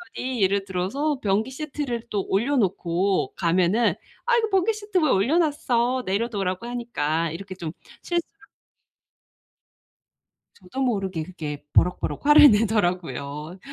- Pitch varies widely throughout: Yes, wide, 6.6 semitones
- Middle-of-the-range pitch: No, high, 205 Hz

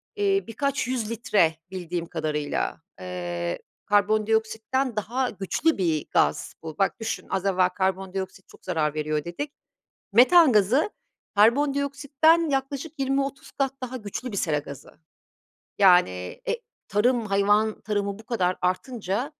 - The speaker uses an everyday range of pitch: No, wide, 6.4 semitones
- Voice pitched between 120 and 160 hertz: No, high, 210 Hz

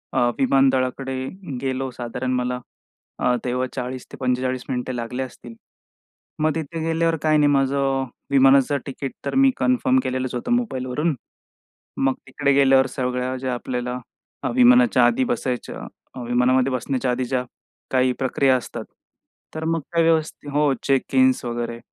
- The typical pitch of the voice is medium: No, low, 130 Hz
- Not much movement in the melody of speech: Yes, narrow, 2.1 semitones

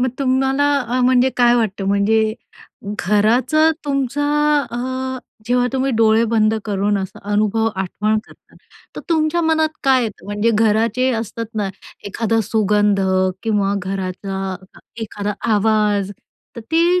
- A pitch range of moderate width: Yes, average, 3.8 semitones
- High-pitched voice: Yes, high, 220 Hz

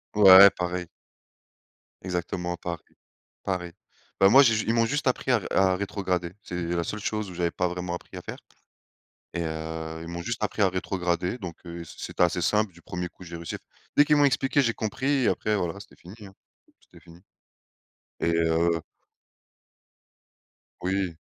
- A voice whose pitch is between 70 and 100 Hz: Yes, very low, 90 Hz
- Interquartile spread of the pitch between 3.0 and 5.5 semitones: Yes, average, 3.6 semitones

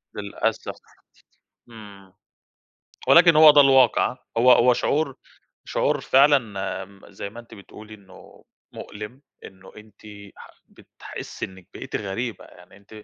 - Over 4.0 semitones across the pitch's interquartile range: Yes, average, 4.9 semitones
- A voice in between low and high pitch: No, low, 110 Hz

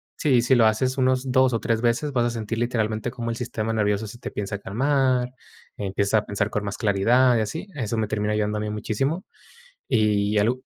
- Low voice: Yes, low, 115 Hz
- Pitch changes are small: No, average, 3.2 semitones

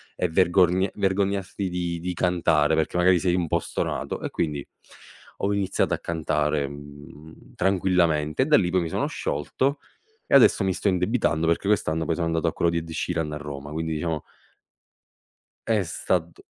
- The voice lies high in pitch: No, very low, 85 Hz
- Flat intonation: No, average, 3.0 semitones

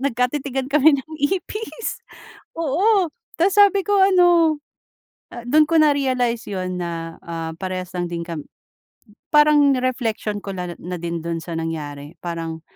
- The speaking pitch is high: Yes, high, 245 Hz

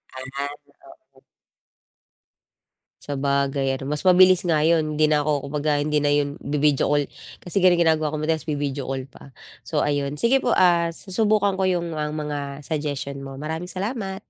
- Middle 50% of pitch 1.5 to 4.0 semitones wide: Yes, average, 3.3 semitones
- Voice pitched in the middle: Yes, medium, 150 Hz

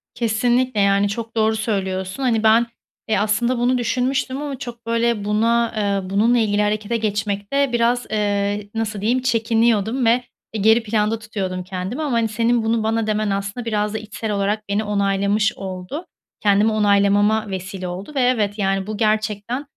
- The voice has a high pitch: Yes, high, 215 Hz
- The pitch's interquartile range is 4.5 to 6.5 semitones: No, narrow, 2.5 semitones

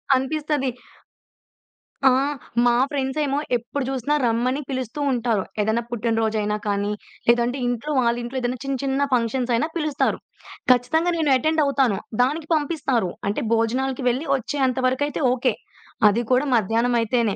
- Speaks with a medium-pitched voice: No, very high, 250 Hz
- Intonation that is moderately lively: Yes, average, 3.1 semitones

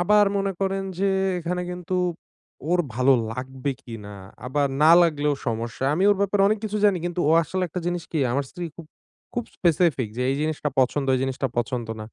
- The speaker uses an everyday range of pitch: No, wide, 5.8 semitones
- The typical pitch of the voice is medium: Yes, medium, 160 Hz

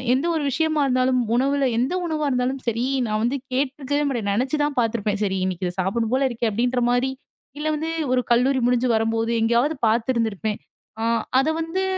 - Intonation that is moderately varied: Yes, average, 3.3 semitones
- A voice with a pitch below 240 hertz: No, very high, 250 Hz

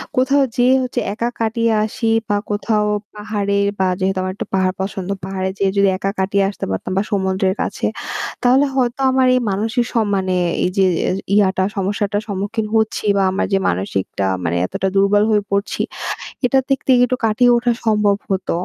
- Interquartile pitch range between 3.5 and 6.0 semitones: No, average, 3.1 semitones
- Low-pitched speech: No, high, 205 Hz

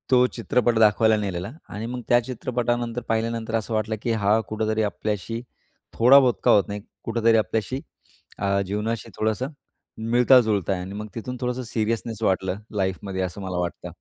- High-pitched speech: No, low, 110 Hz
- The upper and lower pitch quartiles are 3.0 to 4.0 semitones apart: No, narrow, 2.6 semitones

